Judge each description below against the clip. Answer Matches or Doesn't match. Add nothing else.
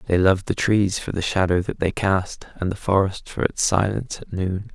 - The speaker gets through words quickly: Matches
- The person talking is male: Matches